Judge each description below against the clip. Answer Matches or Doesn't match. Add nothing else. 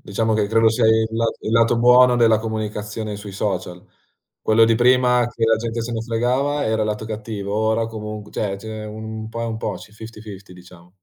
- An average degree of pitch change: Doesn't match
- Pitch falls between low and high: Doesn't match